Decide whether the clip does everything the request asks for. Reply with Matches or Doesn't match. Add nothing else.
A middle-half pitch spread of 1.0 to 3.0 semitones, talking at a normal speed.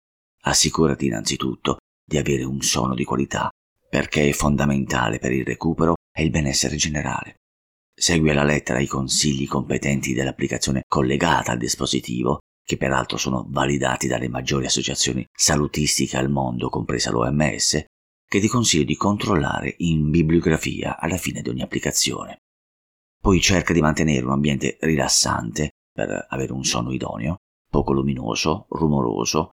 Matches